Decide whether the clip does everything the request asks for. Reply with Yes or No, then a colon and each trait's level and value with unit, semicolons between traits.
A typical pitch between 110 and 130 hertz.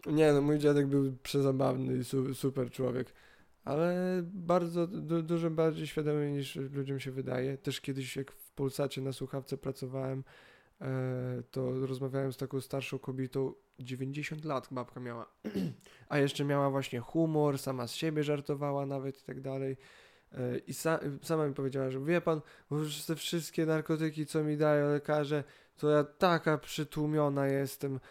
No: medium, 140 Hz